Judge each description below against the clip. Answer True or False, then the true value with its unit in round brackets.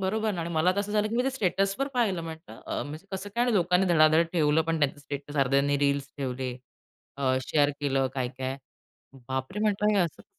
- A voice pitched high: False (160 Hz)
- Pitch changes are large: True (5.9 semitones)